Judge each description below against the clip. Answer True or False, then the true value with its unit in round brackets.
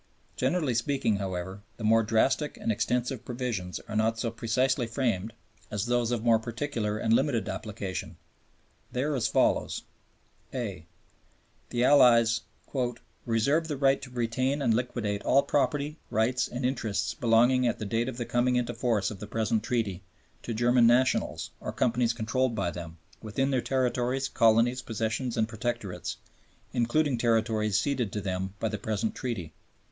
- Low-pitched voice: True (115 Hz)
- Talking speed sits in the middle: True (155 wpm)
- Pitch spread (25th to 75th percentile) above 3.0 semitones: False (2.7 semitones)